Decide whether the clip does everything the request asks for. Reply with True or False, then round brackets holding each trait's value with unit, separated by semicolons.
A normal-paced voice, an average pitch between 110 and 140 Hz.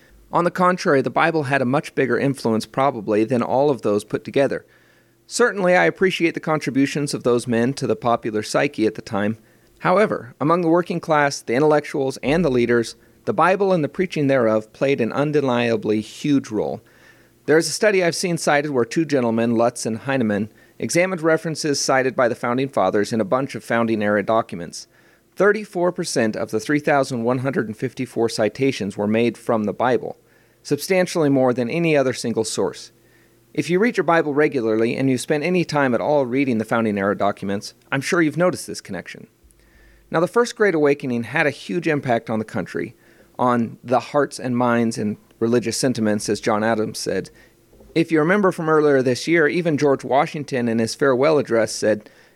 True (185 wpm; 135 Hz)